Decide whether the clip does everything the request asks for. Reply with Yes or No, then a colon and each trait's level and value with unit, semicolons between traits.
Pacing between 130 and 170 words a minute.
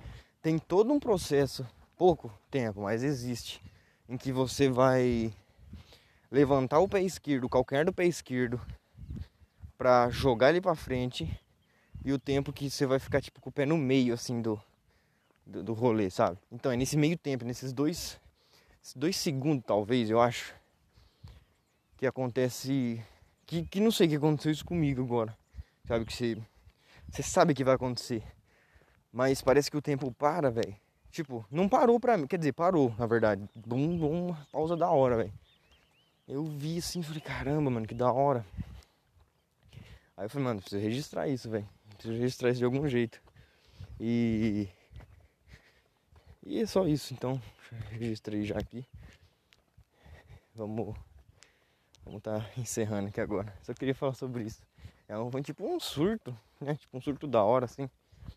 Yes: average, 160 wpm